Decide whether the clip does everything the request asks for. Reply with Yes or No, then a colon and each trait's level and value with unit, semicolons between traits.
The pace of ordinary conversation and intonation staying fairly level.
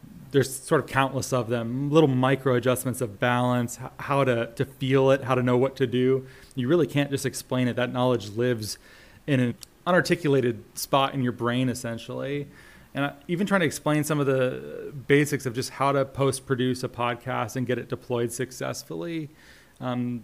Yes: average, 185 wpm; narrow, 1.9 semitones